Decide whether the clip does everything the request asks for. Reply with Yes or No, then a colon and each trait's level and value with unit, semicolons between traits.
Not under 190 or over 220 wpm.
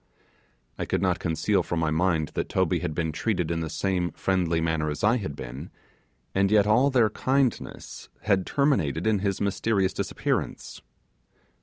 No: average, 160 wpm